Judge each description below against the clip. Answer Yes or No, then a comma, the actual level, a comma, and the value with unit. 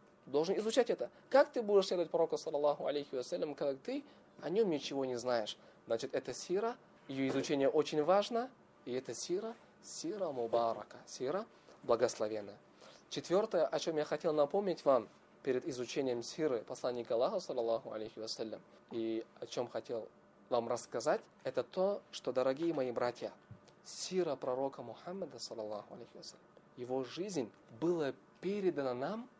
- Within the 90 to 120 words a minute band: No, average, 140 wpm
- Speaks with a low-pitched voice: No, medium, 145 Hz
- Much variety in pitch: Yes, wide, 7.1 semitones